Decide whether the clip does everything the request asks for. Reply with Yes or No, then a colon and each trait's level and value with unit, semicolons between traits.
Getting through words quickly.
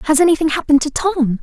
Yes: fast, 210 wpm